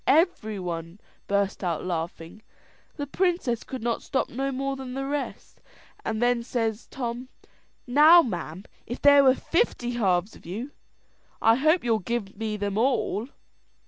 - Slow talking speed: No, average, 150 wpm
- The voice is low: No, high, 235 Hz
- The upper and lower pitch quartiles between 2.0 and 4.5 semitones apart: No, average, 5.1 semitones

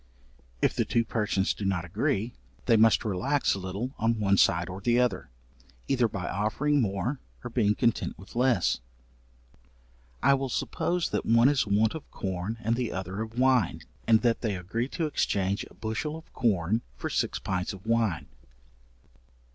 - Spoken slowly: No, average, 170 wpm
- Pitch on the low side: Yes, low, 110 Hz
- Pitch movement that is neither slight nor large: Yes, average, 4.0 semitones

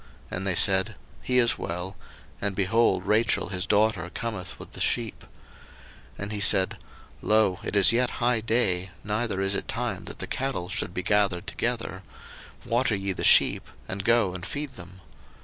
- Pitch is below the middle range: Yes, low, 100 Hz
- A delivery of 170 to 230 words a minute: Yes, average, 175 wpm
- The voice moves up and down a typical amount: Yes, average, 3.7 semitones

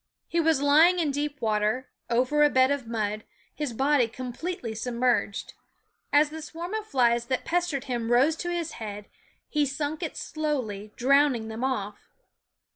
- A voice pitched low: No, very high, 265 Hz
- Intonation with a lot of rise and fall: No, average, 4.4 semitones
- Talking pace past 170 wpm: No, average, 160 wpm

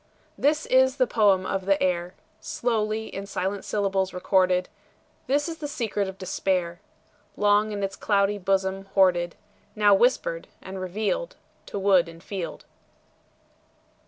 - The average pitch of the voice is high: Yes, high, 195 Hz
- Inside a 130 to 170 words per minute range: Yes, slow, 135 wpm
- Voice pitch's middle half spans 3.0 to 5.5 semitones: No, narrow, 2.5 semitones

